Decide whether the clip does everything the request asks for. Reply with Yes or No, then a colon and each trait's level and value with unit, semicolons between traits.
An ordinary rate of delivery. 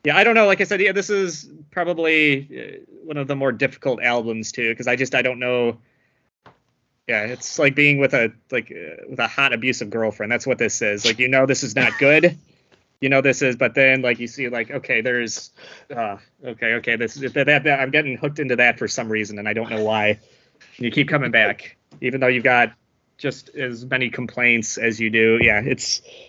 No: fast, 225 wpm